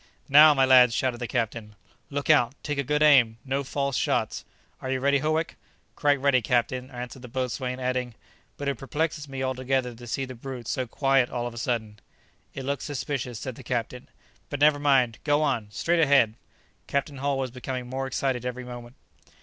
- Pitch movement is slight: Yes, narrow, 2.3 semitones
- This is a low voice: Yes, low, 130 Hz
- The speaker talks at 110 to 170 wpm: No, average, 190 wpm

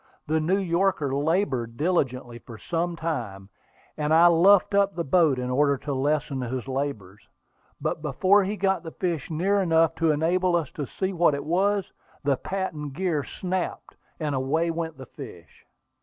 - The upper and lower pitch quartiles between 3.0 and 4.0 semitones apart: No, average, 4.8 semitones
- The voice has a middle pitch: Yes, medium, 160 Hz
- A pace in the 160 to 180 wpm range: Yes, average, 170 wpm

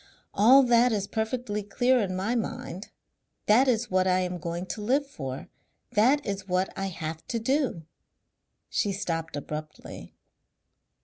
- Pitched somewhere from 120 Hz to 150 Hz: No, high, 205 Hz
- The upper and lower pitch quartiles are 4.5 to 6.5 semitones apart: Yes, average, 4.9 semitones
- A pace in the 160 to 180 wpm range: No, average, 145 wpm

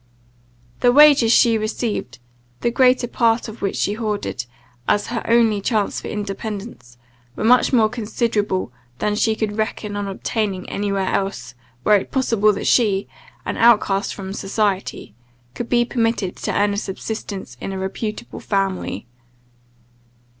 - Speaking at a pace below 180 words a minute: Yes, average, 145 wpm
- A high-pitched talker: Yes, high, 210 Hz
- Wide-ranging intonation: No, average, 2.8 semitones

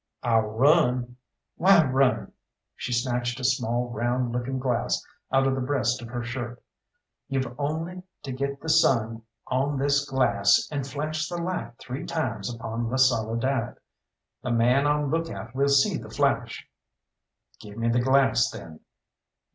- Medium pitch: No, low, 130 Hz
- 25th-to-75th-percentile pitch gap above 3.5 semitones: No, average, 2.9 semitones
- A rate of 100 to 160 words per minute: Yes, average, 155 wpm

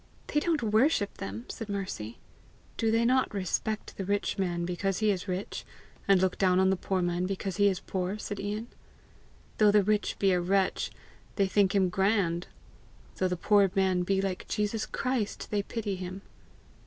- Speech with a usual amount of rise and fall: No, narrow, 2.3 semitones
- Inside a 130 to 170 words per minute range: No, average, 180 wpm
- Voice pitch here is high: Yes, high, 195 Hz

